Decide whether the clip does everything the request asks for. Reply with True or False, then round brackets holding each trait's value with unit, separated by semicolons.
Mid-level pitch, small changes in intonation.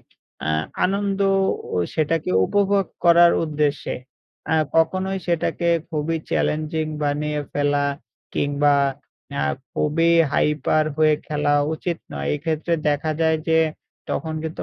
True (155 Hz; 2.3 semitones)